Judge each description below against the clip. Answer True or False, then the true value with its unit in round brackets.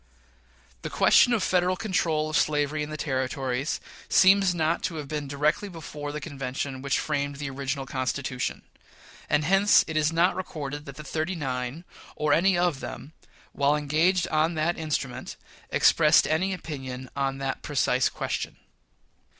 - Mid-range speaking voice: True (150 Hz)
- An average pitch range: True (3.2 semitones)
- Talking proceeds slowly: False (155 wpm)